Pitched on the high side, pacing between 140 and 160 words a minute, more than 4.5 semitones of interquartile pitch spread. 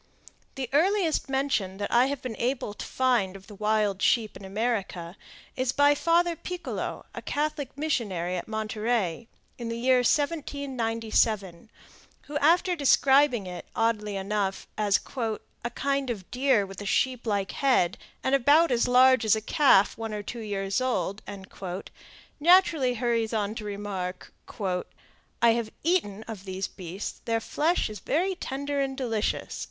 Yes: high, 230 Hz; average, 150 wpm; average, 5.1 semitones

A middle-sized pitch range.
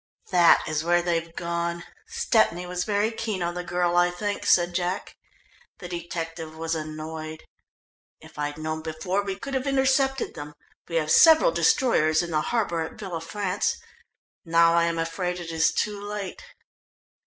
Yes: average, 3.7 semitones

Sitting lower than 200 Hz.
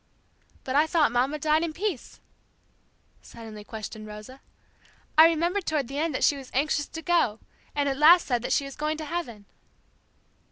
No: very high, 290 Hz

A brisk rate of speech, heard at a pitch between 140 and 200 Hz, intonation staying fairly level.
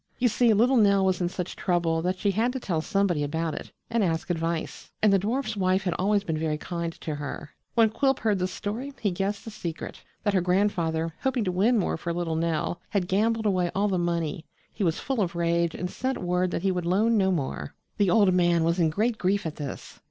No: fast, 235 wpm; medium, 185 Hz; average, 3.7 semitones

